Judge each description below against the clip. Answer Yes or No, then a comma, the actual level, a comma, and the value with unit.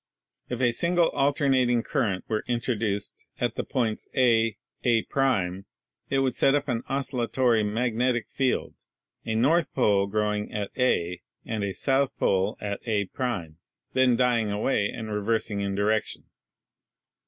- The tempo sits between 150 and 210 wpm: No, average, 140 wpm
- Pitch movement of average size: Yes, average, 3.5 semitones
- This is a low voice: Yes, low, 115 Hz